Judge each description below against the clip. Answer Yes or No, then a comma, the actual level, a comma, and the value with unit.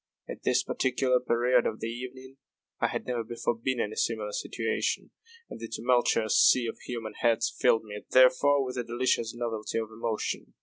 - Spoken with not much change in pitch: Yes, narrow, 2.1 semitones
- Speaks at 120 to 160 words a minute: No, average, 180 wpm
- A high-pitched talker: No, low, 120 Hz